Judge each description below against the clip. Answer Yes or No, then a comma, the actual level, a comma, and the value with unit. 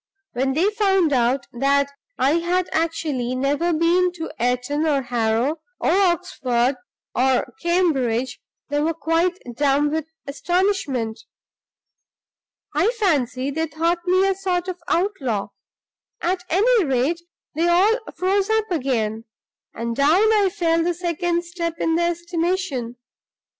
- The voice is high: Yes, very high, 330 Hz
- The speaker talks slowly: Yes, slow, 130 wpm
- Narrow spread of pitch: No, average, 5.2 semitones